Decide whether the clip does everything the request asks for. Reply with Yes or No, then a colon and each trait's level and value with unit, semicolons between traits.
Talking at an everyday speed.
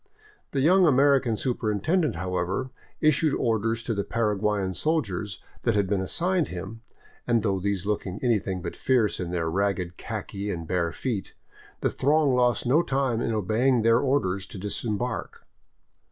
Yes: average, 155 wpm